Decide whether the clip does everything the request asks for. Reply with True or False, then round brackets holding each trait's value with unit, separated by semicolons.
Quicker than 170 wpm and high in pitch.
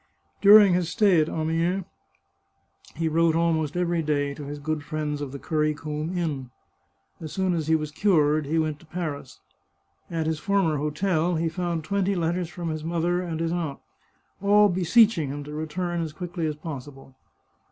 False (180 wpm; 160 Hz)